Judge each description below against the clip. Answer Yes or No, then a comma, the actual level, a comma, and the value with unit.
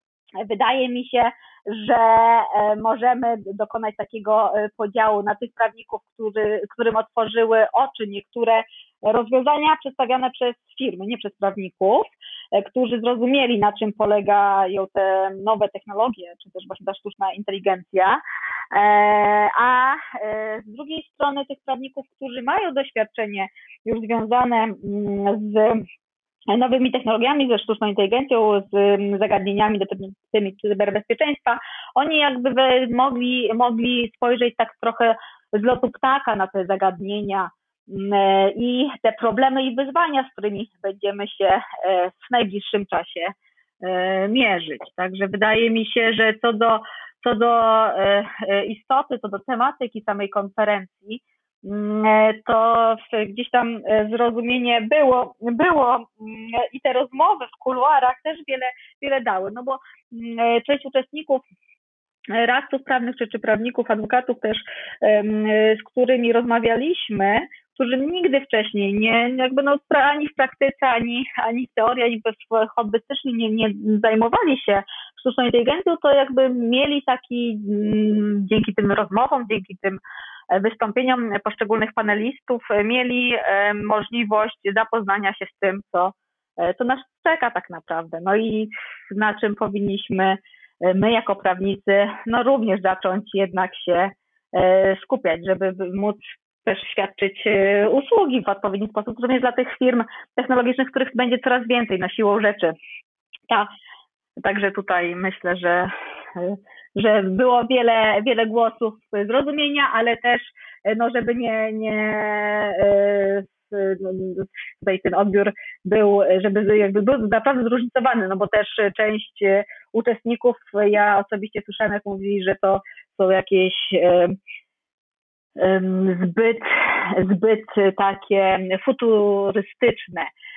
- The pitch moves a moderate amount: Yes, average, 3.6 semitones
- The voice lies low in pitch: No, high, 220 Hz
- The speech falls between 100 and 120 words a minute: Yes, average, 115 wpm